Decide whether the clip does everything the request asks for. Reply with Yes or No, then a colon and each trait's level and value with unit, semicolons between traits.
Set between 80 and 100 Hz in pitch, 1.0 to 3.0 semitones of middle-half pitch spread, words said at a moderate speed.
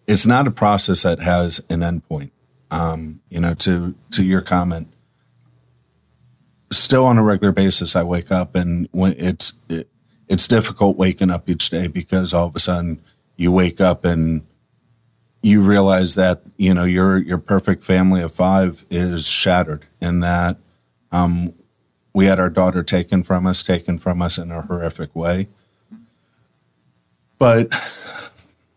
Yes: very low, 90 Hz; narrow, 2.5 semitones; average, 155 wpm